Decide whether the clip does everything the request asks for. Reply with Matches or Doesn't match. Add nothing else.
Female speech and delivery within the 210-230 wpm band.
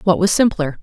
Matches